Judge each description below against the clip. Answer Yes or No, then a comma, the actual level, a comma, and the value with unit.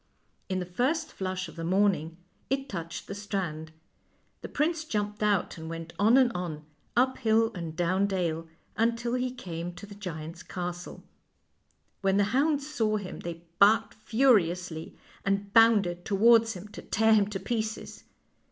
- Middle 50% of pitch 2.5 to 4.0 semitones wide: No, average, 4.4 semitones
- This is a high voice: Yes, high, 200 Hz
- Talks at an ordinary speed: Yes, average, 160 wpm